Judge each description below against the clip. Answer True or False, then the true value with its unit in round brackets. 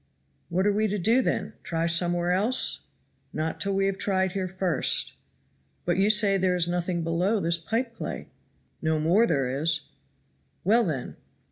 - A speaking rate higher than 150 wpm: True (165 wpm)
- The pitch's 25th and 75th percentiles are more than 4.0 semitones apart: False (3.3 semitones)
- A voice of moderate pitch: True (180 Hz)